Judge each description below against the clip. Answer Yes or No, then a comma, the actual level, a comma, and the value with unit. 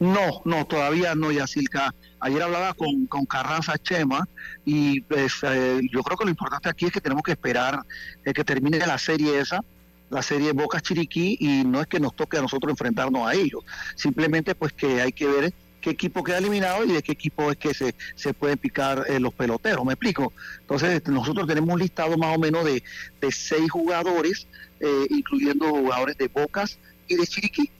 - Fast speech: Yes, fast, 195 wpm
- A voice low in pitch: No, medium, 155 Hz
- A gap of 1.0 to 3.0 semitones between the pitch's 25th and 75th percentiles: No, average, 3.7 semitones